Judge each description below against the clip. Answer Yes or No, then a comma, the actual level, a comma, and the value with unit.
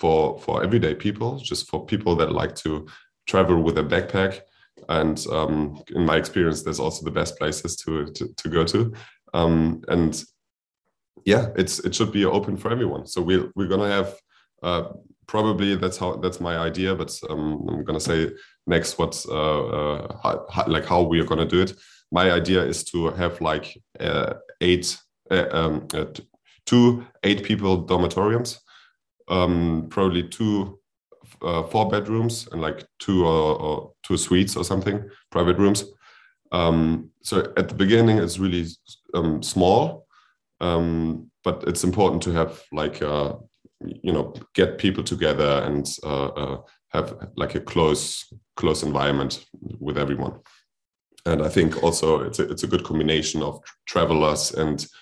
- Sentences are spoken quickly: No, average, 165 wpm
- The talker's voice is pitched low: Yes, very low, 85 Hz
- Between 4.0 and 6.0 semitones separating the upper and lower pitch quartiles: No, average, 3.6 semitones